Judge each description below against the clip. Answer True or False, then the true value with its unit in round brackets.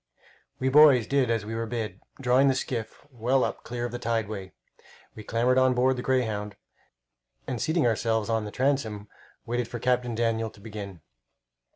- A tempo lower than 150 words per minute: False (175 wpm)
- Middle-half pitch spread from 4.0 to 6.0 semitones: False (2.7 semitones)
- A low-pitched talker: True (115 Hz)